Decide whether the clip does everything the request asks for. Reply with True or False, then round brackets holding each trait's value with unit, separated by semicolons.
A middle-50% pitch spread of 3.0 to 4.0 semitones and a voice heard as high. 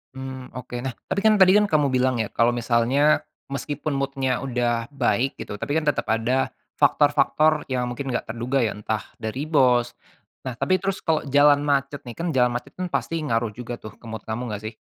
False (3.4 semitones; 130 Hz)